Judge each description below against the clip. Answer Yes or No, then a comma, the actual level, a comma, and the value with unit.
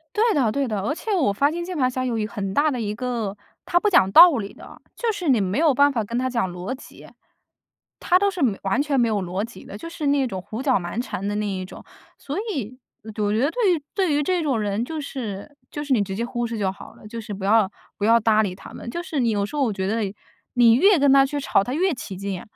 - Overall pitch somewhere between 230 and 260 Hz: Yes, high, 240 Hz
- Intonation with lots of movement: Yes, wide, 6.1 semitones